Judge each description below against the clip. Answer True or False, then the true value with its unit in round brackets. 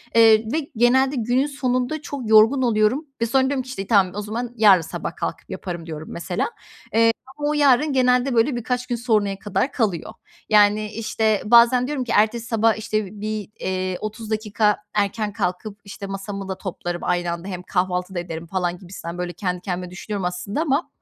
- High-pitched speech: True (215 Hz)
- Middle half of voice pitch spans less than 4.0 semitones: False (4.6 semitones)